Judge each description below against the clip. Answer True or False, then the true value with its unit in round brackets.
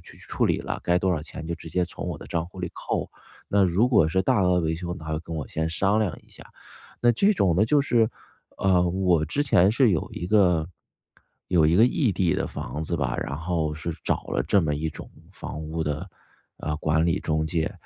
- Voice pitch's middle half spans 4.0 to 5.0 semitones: False (3.4 semitones)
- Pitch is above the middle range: False (85 Hz)